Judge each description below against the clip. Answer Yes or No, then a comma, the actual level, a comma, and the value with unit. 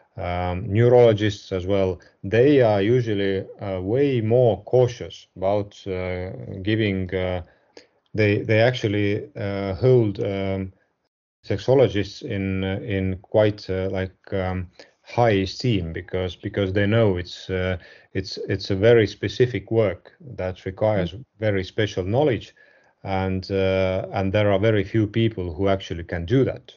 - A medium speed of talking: No, slow, 130 wpm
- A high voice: No, low, 100 Hz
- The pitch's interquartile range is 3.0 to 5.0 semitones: No, narrow, 2.6 semitones